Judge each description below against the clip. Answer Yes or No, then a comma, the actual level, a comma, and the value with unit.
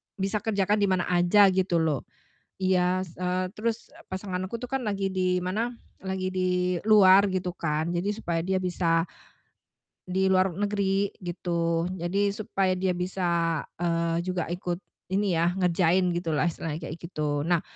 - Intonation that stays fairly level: Yes, narrow, 2.0 semitones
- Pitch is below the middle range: No, medium, 185 Hz